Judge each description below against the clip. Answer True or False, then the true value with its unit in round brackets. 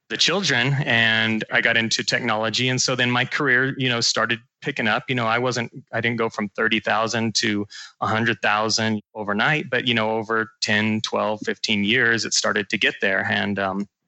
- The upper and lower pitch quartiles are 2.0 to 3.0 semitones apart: True (2.4 semitones)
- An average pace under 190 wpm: False (195 wpm)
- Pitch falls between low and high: False (115 Hz)